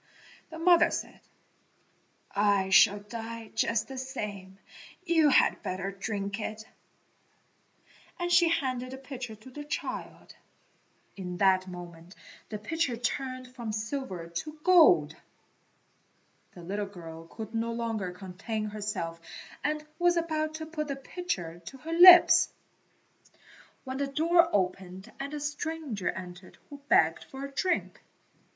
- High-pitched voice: Yes, high, 230 Hz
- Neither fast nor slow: No, slow, 130 wpm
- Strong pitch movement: Yes, wide, 7.3 semitones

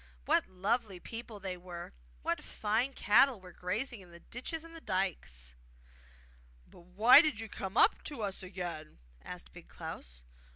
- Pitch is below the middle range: No, high, 195 Hz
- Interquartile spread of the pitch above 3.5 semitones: Yes, average, 4.7 semitones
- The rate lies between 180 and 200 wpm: No, average, 160 wpm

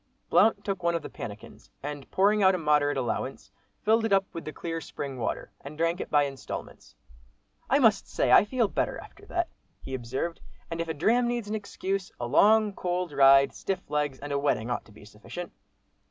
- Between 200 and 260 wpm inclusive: Yes, fast, 205 wpm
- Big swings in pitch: Yes, wide, 6.4 semitones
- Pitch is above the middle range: No, medium, 165 Hz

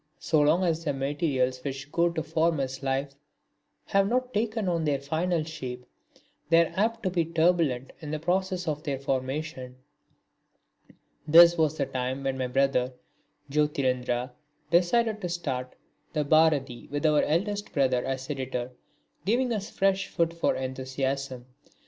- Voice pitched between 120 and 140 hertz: No, medium, 150 Hz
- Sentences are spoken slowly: No, average, 150 wpm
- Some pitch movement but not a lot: Yes, average, 4.4 semitones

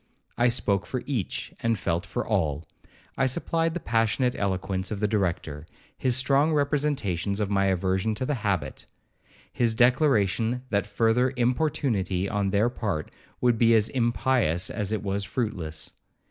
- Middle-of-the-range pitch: No, low, 110 Hz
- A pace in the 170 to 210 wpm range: No, average, 150 wpm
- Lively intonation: No, average, 4.4 semitones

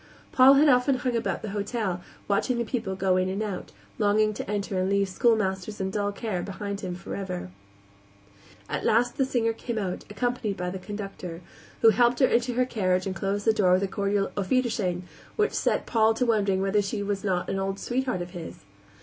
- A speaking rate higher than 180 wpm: Yes, fast, 205 wpm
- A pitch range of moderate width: Yes, average, 3.4 semitones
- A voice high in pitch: Yes, high, 205 Hz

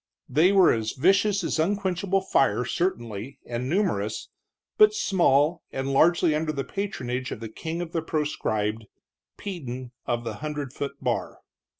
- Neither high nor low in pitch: Yes, medium, 150 Hz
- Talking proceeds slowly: No, average, 150 wpm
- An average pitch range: No, wide, 6.5 semitones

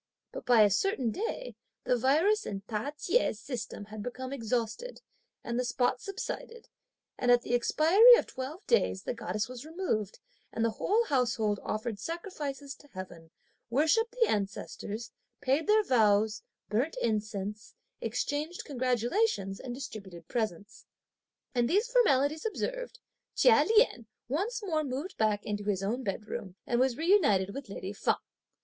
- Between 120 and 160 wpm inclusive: Yes, average, 145 wpm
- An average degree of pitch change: No, wide, 7.6 semitones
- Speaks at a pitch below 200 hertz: No, high, 245 Hz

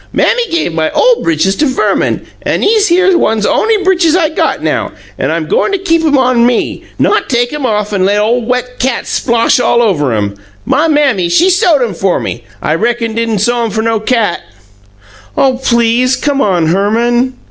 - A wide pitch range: Yes, wide, 6.1 semitones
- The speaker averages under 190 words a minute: No, average, 195 wpm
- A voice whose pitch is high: Yes, high, 240 Hz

